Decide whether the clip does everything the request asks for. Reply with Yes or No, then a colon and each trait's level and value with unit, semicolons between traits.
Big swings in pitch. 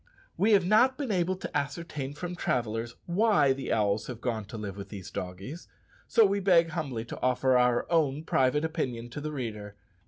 Yes: wide, 6.7 semitones